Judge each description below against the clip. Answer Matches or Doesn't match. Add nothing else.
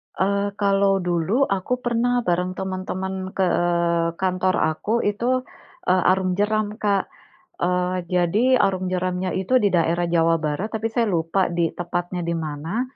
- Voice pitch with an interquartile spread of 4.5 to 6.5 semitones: Doesn't match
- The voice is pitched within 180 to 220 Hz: Matches